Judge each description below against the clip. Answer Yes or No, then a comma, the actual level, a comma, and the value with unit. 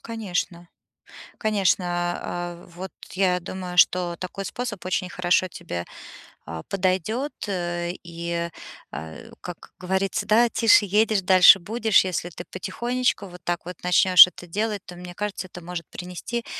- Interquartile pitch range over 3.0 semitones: No, narrow, 2.5 semitones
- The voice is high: No, medium, 180 Hz